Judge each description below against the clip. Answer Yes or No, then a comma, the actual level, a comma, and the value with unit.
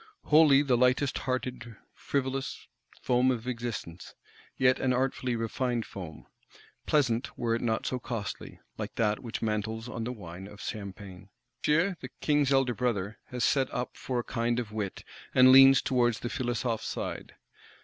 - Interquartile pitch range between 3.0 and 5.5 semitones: No, narrow, 2.6 semitones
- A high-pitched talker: No, low, 120 Hz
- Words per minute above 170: No, average, 160 wpm